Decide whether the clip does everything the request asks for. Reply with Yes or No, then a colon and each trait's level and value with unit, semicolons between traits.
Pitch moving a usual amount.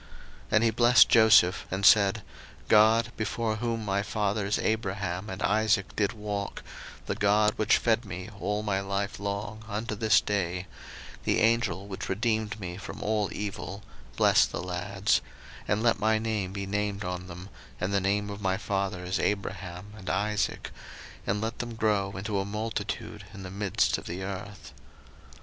No: narrow, 1.9 semitones